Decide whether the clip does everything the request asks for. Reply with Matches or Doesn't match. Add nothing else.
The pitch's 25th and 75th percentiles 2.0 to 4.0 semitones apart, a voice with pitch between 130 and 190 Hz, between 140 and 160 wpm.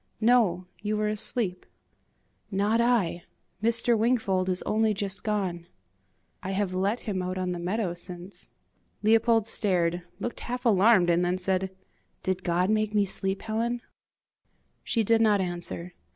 Doesn't match